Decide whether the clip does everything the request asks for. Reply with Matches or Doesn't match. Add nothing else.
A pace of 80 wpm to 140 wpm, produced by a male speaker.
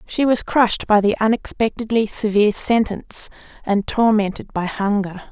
Doesn't match